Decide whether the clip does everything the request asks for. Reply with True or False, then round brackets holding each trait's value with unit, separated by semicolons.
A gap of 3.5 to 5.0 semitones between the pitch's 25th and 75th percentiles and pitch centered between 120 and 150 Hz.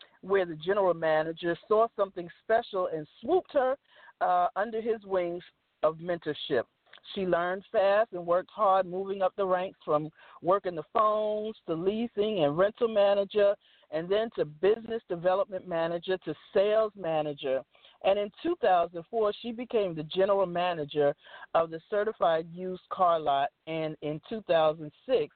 False (4.0 semitones; 185 Hz)